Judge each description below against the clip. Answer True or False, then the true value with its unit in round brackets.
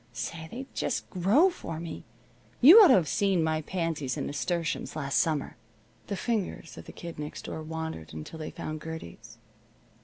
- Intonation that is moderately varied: True (3.4 semitones)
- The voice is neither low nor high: True (160 Hz)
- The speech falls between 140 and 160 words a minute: False (175 wpm)